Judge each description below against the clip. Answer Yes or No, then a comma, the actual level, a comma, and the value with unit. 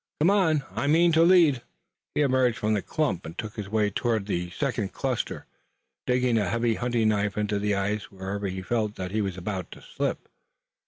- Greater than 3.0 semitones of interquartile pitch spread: Yes, average, 4.4 semitones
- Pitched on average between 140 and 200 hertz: No, low, 110 Hz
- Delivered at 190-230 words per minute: Yes, average, 200 wpm